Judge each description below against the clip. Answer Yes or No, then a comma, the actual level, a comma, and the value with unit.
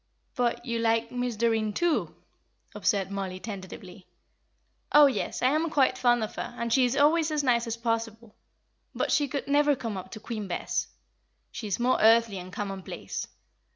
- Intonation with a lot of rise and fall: No, average, 3.7 semitones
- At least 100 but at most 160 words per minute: No, average, 175 wpm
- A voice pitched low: No, high, 230 Hz